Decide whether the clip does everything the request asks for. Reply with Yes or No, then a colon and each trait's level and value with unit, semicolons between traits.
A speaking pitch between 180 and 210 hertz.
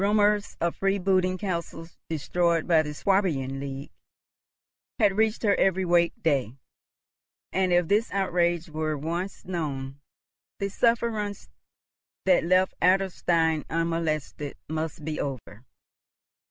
No: medium, 170 Hz